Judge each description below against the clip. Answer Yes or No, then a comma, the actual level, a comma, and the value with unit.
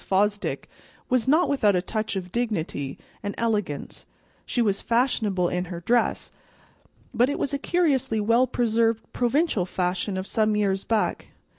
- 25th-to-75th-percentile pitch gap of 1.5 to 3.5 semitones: No, average, 4.2 semitones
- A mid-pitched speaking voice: No, high, 215 Hz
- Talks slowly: No, average, 150 wpm